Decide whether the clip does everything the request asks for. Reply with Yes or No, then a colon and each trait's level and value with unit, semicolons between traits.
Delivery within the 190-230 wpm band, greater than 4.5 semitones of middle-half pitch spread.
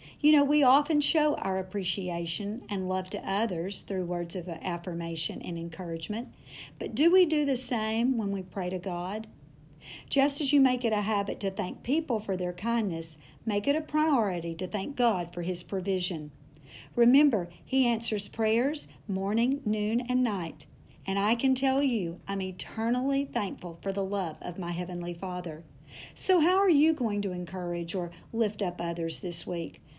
No: average, 175 wpm; wide, 5.6 semitones